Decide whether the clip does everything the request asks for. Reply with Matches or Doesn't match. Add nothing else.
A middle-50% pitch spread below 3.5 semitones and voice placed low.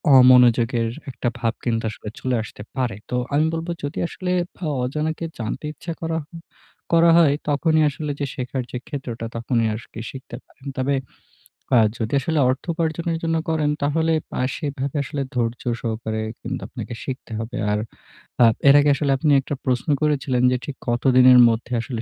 Doesn't match